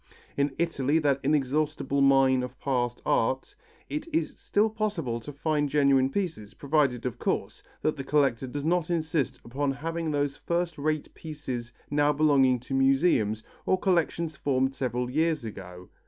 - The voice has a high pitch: No, medium, 140 Hz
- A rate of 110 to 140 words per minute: No, average, 155 wpm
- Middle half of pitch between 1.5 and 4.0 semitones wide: Yes, average, 3.2 semitones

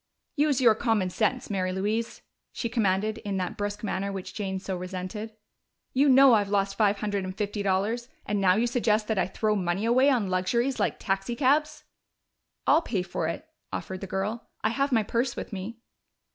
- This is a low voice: No, high, 210 Hz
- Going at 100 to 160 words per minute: No, average, 185 wpm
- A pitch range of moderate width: Yes, average, 3.6 semitones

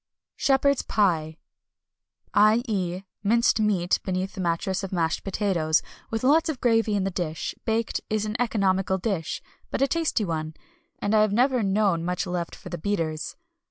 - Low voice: No, high, 195 Hz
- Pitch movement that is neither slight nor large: Yes, average, 4.1 semitones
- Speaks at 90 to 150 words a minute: No, average, 160 wpm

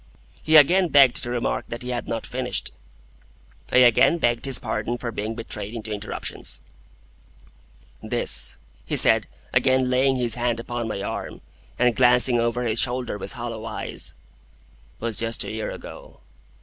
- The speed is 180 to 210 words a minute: No, average, 155 wpm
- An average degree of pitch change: No, narrow, 1.9 semitones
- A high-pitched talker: No, low, 120 Hz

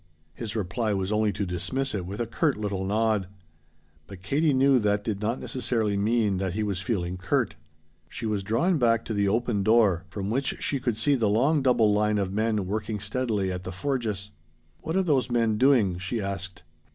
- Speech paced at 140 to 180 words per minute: No, average, 200 wpm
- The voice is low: Yes, low, 105 Hz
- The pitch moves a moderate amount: Yes, average, 3.5 semitones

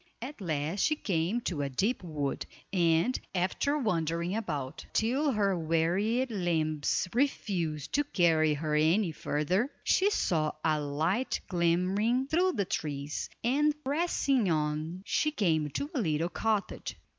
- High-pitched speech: No, medium, 180 Hz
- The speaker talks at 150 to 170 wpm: No, slow, 135 wpm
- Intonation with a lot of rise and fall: Yes, wide, 7.1 semitones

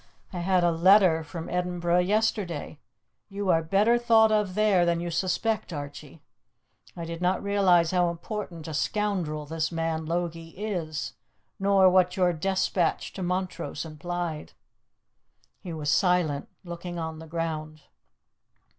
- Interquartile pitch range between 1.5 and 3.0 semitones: Yes, average, 2.7 semitones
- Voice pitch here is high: No, medium, 175 Hz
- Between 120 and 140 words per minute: Yes, slow, 135 wpm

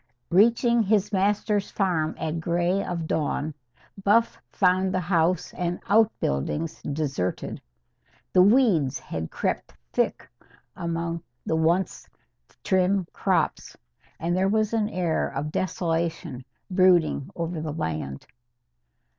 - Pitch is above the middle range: No, medium, 175 Hz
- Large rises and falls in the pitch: No, average, 3.5 semitones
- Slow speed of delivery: Yes, slow, 115 wpm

